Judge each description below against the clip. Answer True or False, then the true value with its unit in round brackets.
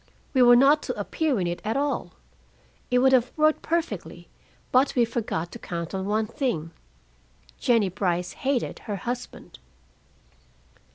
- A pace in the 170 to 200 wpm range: False (150 wpm)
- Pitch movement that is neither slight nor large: False (5.7 semitones)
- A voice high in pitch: True (240 Hz)